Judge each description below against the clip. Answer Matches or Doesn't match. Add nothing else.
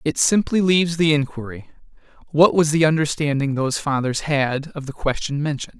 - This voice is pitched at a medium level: Matches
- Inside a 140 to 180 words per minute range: Matches